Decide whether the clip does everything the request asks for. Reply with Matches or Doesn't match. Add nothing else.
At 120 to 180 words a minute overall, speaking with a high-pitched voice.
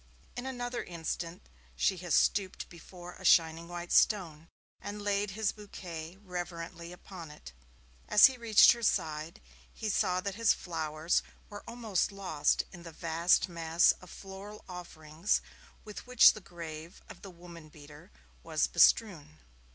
Doesn't match